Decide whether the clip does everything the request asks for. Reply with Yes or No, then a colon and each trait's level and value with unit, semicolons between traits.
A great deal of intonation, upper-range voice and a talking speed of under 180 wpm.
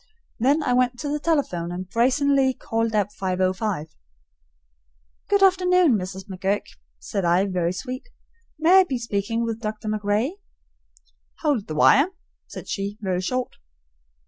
Yes: wide, 6.5 semitones; high, 225 Hz; average, 140 wpm